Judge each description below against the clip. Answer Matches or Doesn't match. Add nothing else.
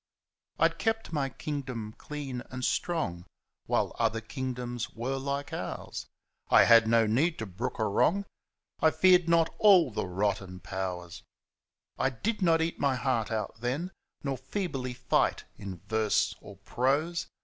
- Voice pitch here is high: Doesn't match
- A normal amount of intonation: Doesn't match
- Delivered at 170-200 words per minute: Doesn't match